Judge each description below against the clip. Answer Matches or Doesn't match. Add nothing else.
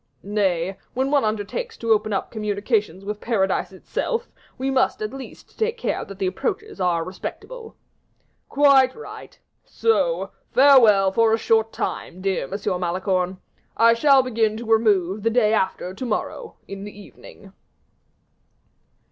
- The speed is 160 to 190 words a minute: Doesn't match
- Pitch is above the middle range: Matches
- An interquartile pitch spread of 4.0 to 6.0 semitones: Matches